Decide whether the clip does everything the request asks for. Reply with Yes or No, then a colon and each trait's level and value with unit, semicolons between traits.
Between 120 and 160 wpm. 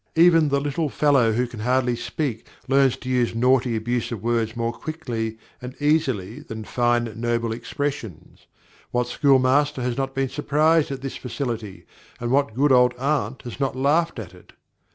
No: average, 170 wpm